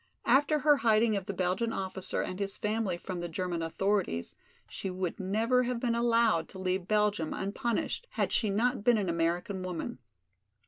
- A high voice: Yes, high, 200 Hz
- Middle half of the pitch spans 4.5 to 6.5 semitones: No, average, 4.0 semitones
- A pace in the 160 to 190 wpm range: Yes, average, 175 wpm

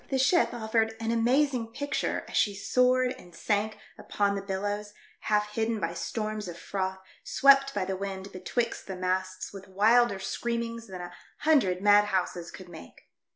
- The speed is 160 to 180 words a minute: Yes, average, 165 wpm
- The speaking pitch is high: Yes, high, 210 Hz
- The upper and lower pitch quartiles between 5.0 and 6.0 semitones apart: No, average, 3.6 semitones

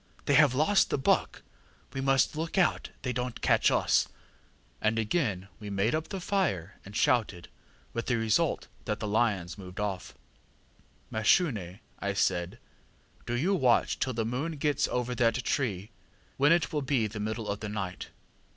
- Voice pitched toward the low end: Yes, low, 115 Hz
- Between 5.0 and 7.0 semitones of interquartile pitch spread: Yes, wide, 5.4 semitones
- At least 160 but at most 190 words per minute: Yes, average, 170 wpm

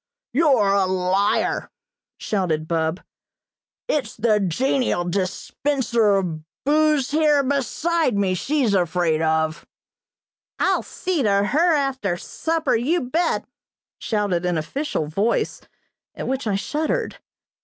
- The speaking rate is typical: No, slow, 110 wpm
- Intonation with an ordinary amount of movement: No, wide, 7.9 semitones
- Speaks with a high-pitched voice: Yes, high, 215 Hz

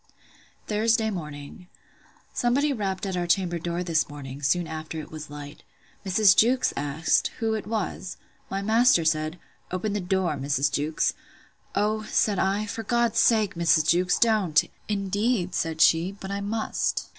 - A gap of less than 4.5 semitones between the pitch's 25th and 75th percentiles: No, average, 5.0 semitones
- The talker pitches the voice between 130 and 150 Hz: No, high, 190 Hz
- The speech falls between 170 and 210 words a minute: No, average, 155 wpm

